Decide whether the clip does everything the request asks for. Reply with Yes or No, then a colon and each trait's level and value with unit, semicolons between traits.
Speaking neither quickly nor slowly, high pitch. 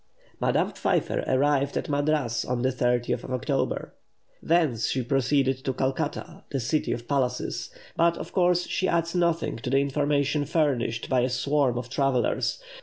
No: average, 160 wpm; low, 135 Hz